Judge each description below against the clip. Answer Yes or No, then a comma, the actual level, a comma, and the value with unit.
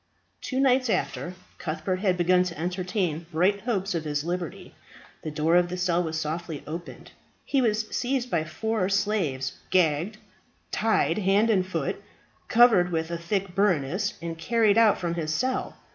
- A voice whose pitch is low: No, medium, 180 Hz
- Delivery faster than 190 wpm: No, average, 160 wpm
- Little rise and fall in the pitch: No, average, 4.3 semitones